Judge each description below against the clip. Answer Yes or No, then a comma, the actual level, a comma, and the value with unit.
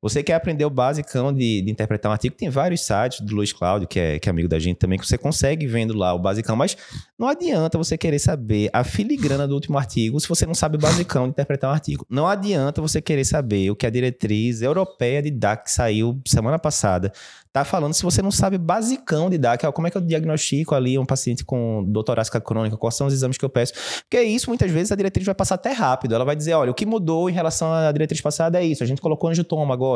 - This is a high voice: No, medium, 140 Hz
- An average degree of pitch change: No, wide, 5.8 semitones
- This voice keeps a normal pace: No, fast, 250 wpm